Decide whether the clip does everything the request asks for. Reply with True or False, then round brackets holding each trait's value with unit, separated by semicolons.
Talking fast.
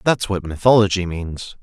False (150 wpm)